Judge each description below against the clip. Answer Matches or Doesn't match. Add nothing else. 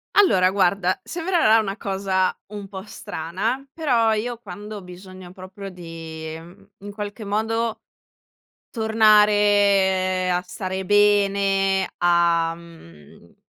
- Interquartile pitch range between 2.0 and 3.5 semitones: Matches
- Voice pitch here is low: Doesn't match